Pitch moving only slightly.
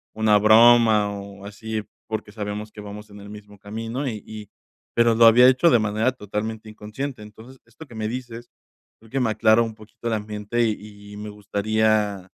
Yes: narrow, 1.8 semitones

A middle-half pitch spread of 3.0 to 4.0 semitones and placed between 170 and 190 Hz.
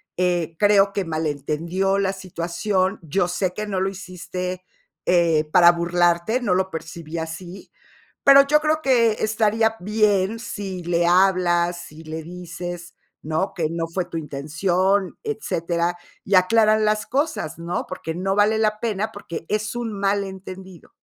Yes: average, 3.3 semitones; medium, 185 Hz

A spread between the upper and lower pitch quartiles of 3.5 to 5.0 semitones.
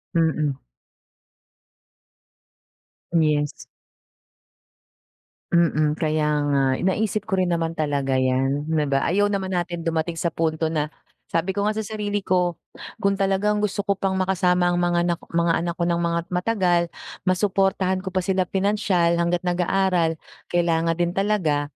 No: average, 2.8 semitones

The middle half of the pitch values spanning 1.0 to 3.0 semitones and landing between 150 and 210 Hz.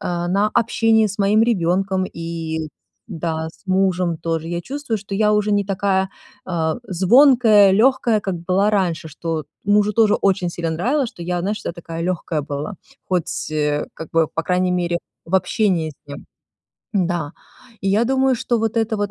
No: average, 4.1 semitones; high, 190 Hz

